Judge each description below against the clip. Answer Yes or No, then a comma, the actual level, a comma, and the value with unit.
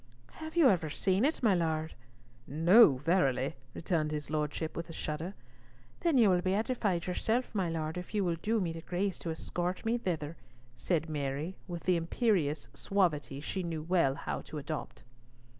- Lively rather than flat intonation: No, average, 3.9 semitones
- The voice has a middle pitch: Yes, medium, 170 Hz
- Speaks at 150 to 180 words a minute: Yes, average, 175 wpm